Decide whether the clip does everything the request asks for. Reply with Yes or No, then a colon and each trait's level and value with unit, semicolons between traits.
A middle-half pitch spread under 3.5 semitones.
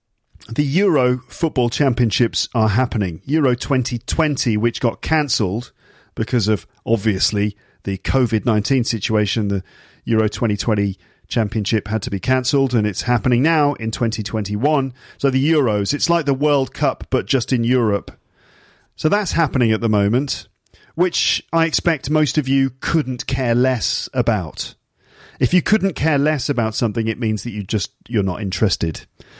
No: average, 4.2 semitones